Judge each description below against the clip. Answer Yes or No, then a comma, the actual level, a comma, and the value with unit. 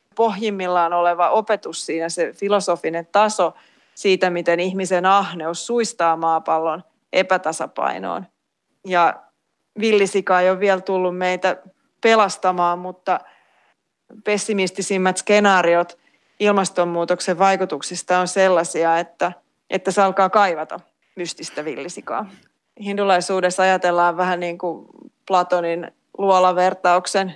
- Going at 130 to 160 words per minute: No, slow, 95 wpm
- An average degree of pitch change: No, narrow, 2.1 semitones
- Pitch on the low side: No, medium, 185 Hz